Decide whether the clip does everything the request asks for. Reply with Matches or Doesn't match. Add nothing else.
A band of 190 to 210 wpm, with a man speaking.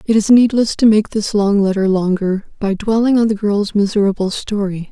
Doesn't match